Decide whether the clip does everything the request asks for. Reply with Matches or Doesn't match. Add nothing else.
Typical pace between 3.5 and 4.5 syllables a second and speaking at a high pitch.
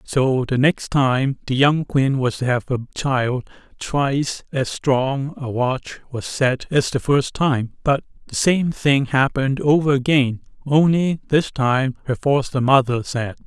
Doesn't match